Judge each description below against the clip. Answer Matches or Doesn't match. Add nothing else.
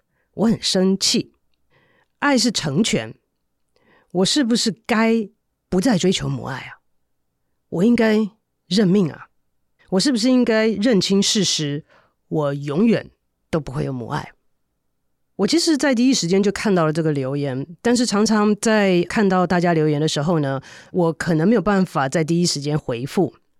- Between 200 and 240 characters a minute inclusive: Matches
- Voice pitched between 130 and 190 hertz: Matches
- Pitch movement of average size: Doesn't match